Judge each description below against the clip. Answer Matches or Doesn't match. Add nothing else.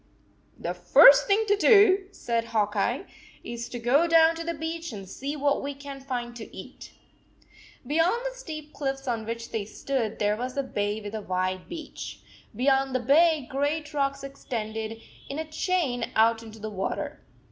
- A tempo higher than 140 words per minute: Matches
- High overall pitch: Matches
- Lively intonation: Matches